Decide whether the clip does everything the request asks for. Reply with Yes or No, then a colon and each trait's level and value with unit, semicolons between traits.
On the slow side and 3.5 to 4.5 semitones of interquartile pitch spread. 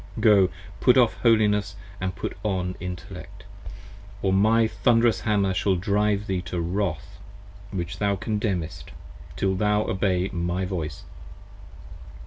No: slow, 120 wpm; narrow, 2.4 semitones